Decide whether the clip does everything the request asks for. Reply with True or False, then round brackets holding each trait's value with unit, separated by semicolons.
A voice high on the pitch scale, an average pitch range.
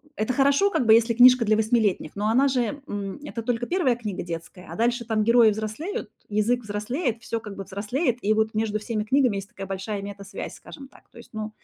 True (220 Hz; 3.0 semitones)